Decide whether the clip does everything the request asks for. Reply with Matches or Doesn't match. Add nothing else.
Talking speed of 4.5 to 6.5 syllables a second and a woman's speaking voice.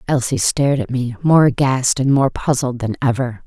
Matches